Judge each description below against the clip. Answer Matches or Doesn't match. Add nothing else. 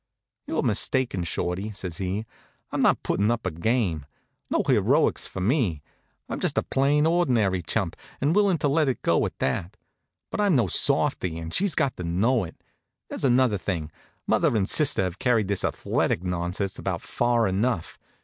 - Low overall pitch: Matches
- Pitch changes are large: Matches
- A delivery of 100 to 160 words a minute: Doesn't match